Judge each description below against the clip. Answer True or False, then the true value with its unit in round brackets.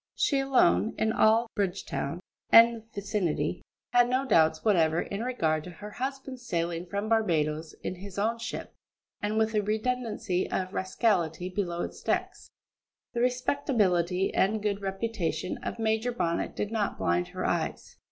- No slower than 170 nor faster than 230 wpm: False (150 wpm)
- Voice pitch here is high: True (205 Hz)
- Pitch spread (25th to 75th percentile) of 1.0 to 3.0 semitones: False (4.7 semitones)